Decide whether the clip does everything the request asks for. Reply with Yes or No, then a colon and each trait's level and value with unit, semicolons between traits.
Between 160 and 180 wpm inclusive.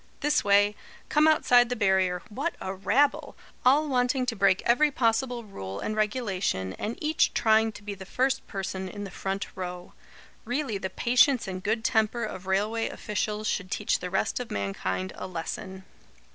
Yes: average, 175 wpm